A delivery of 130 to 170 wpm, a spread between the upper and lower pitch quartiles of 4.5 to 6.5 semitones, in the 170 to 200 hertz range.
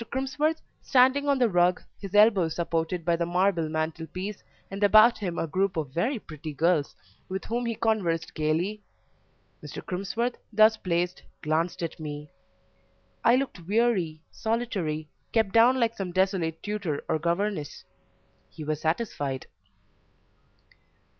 Yes: slow, 135 wpm; wide, 5.4 semitones; medium, 185 Hz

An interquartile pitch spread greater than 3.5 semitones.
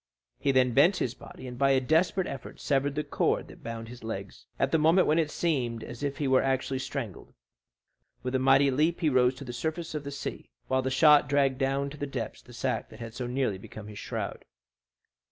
No: average, 2.7 semitones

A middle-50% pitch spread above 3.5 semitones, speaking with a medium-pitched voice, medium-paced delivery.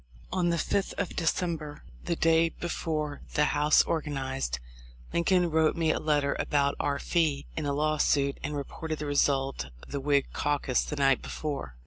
No: narrow, 2.5 semitones; medium, 150 Hz; average, 170 wpm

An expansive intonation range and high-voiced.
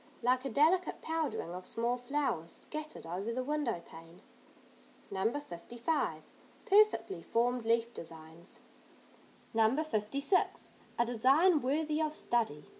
Yes: wide, 7.0 semitones; high, 240 Hz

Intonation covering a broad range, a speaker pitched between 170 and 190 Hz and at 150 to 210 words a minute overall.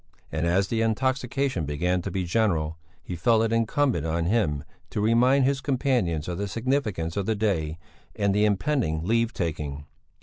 No: wide, 5.9 semitones; low, 100 Hz; average, 170 wpm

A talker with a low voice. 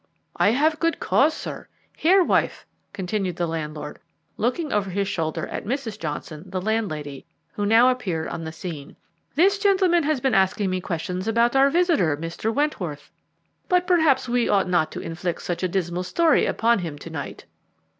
No: high, 200 Hz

